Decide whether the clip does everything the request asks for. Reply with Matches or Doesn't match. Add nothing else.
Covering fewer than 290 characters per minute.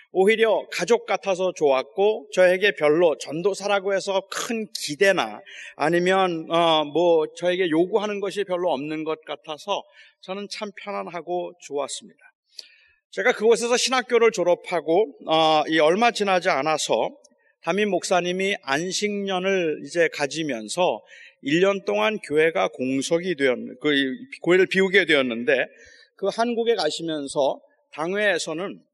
Matches